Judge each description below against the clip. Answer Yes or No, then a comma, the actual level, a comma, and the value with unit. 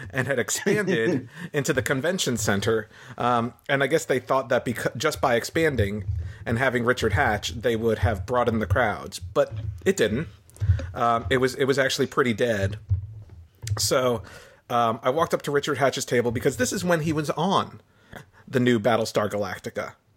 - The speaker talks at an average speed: Yes, average, 175 wpm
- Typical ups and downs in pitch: Yes, average, 4.4 semitones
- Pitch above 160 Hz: No, low, 120 Hz